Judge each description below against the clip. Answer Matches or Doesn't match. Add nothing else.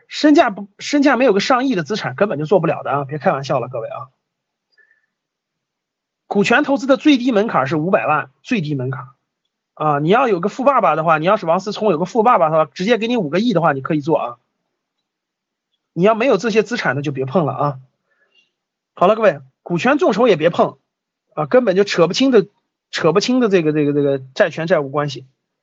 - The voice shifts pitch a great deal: Matches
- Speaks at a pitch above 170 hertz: Matches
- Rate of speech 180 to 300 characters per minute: Doesn't match